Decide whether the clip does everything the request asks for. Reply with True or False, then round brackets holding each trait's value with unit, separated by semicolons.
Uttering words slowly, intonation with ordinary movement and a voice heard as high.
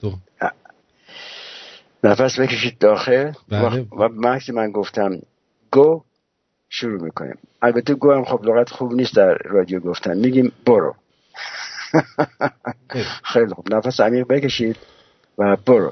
False (105 wpm; 3.6 semitones; 120 Hz)